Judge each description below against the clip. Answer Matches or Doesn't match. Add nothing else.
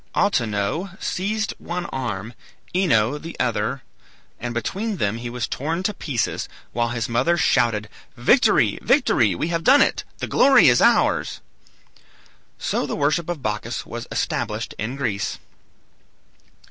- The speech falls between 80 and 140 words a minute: Matches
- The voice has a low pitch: Matches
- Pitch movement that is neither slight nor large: Doesn't match